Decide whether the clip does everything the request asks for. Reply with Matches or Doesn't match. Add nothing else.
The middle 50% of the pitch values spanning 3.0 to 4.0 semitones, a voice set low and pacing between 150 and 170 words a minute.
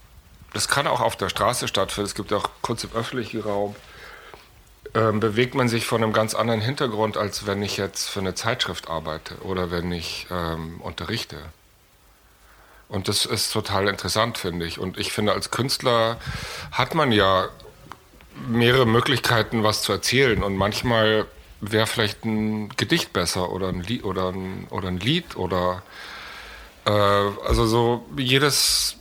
Matches